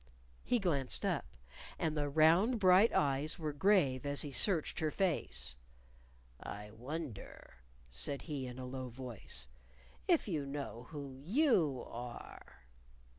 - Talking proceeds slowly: Yes, slow, 130 wpm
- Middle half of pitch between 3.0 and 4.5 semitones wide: No, average, 4.9 semitones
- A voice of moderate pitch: Yes, medium, 145 Hz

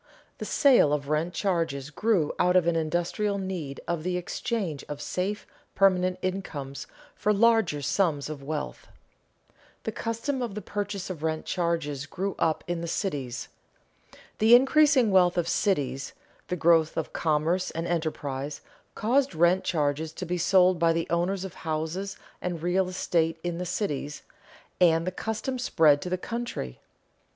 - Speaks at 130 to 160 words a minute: Yes, average, 155 wpm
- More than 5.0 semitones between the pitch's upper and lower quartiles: No, average, 3.8 semitones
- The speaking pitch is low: No, medium, 175 Hz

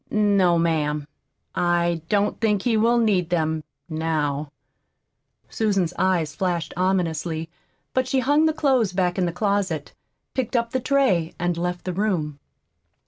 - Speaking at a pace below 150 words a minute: Yes, average, 140 wpm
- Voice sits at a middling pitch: Yes, medium, 180 Hz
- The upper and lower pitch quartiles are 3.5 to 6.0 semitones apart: Yes, average, 4.6 semitones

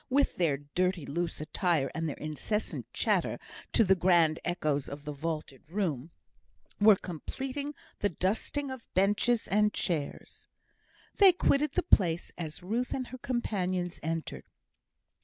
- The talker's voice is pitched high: No, medium, 180 Hz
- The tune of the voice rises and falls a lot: Yes, wide, 5.9 semitones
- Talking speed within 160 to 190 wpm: No, average, 140 wpm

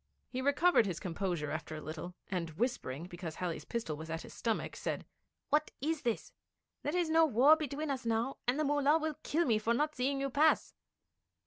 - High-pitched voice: Yes, high, 245 Hz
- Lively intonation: Yes, wide, 8.8 semitones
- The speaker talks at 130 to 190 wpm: No, average, 200 wpm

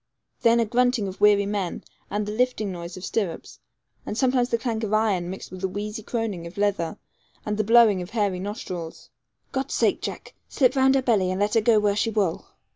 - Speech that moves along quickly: Yes, fast, 210 wpm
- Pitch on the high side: Yes, high, 210 Hz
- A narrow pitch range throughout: No, average, 3.4 semitones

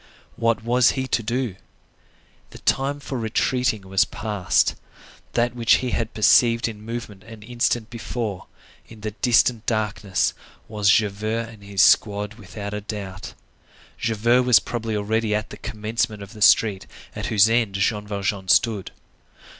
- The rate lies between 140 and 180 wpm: Yes, average, 150 wpm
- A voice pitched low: Yes, low, 110 Hz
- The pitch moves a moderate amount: No, narrow, 2.2 semitones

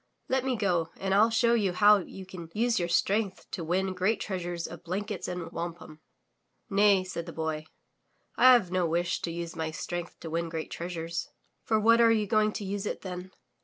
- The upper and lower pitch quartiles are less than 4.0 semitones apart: Yes, average, 3.6 semitones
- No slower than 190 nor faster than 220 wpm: Yes, average, 200 wpm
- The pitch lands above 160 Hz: Yes, medium, 185 Hz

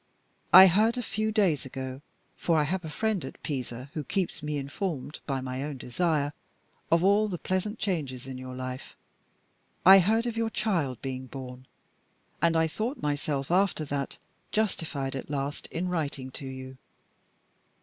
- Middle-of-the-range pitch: Yes, medium, 150 Hz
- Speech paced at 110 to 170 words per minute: Yes, average, 165 wpm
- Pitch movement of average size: No, wide, 6.1 semitones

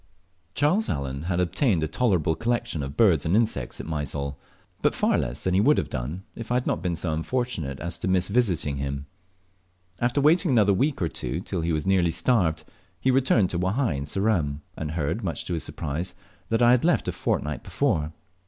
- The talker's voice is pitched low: Yes, very low, 90 Hz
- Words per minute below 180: No, fast, 205 wpm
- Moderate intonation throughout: No, wide, 7.2 semitones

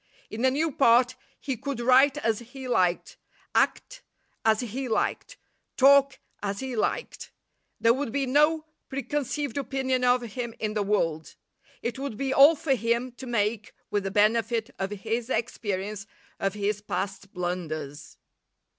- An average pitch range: Yes, average, 4.3 semitones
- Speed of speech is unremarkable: Yes, average, 150 wpm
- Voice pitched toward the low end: No, high, 235 Hz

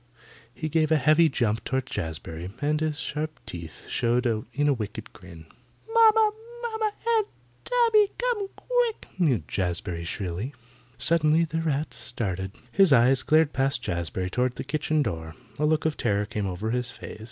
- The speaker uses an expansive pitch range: Yes, wide, 8.0 semitones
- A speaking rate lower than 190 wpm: Yes, average, 160 wpm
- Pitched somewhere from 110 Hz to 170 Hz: Yes, low, 135 Hz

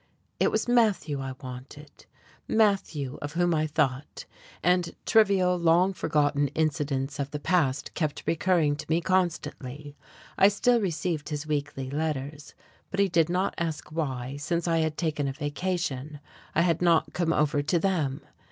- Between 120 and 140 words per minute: No, average, 155 wpm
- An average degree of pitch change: Yes, average, 3.5 semitones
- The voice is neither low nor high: Yes, medium, 155 Hz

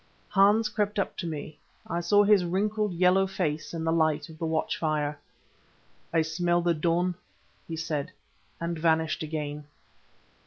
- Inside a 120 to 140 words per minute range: No, average, 155 wpm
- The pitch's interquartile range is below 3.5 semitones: Yes, average, 2.9 semitones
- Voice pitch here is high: No, medium, 165 Hz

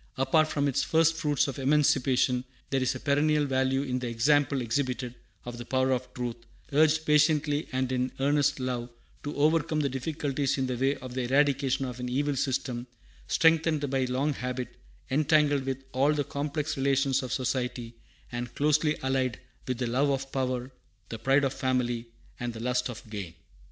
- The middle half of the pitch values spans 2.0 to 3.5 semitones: Yes, narrow, 2.4 semitones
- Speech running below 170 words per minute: No, average, 175 wpm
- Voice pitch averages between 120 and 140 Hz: Yes, low, 135 Hz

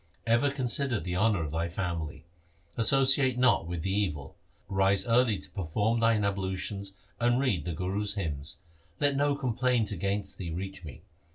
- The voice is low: Yes, low, 100 Hz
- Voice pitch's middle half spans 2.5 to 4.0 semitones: No, average, 5.1 semitones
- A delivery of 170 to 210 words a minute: No, average, 160 wpm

